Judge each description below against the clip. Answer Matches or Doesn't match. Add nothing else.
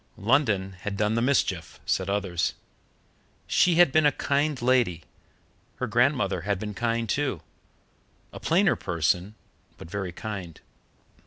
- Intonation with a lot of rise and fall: Matches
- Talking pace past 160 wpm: Doesn't match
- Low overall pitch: Matches